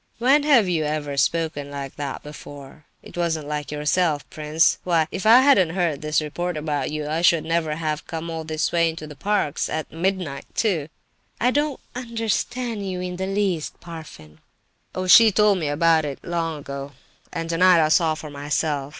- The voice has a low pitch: No, medium, 165 Hz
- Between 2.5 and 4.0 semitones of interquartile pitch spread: Yes, average, 3.7 semitones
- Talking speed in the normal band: Yes, average, 185 wpm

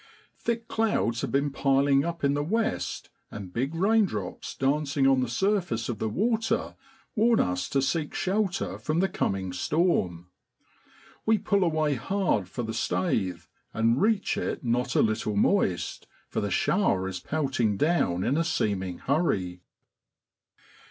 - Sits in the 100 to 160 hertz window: Yes, low, 135 Hz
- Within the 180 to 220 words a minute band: No, average, 150 wpm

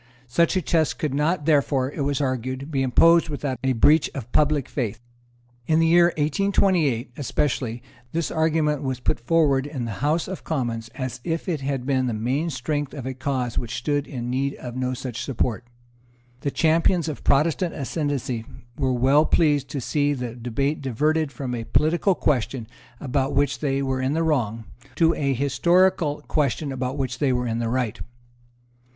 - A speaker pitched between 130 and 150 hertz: Yes, medium, 140 Hz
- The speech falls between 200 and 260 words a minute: No, average, 180 wpm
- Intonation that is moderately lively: Yes, average, 3.4 semitones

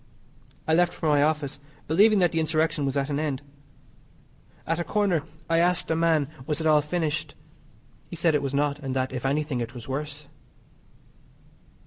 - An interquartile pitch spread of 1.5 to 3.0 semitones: Yes, narrow, 2.5 semitones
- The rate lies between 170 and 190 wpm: Yes, average, 180 wpm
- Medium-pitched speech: Yes, medium, 150 Hz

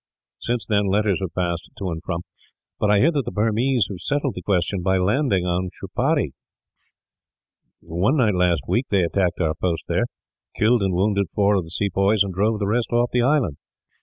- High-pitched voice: No, low, 100 Hz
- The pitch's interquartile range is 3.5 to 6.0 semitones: Yes, average, 3.8 semitones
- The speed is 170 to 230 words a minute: Yes, average, 195 wpm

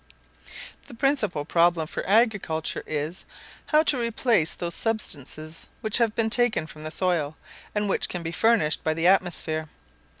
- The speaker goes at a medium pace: Yes, average, 155 wpm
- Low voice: No, medium, 180 Hz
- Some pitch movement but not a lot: No, wide, 6.1 semitones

